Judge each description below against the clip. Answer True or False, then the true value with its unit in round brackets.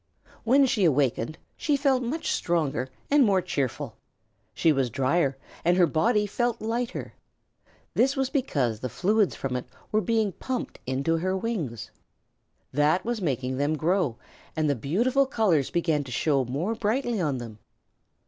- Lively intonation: True (8.8 semitones)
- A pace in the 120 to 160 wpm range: True (155 wpm)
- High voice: False (175 Hz)